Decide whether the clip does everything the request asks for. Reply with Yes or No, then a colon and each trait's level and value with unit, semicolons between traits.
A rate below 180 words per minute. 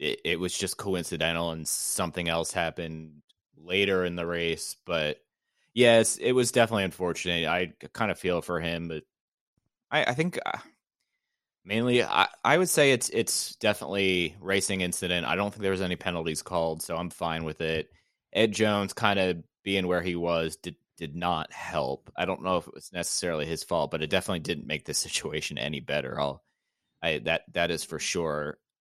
No: average, 185 wpm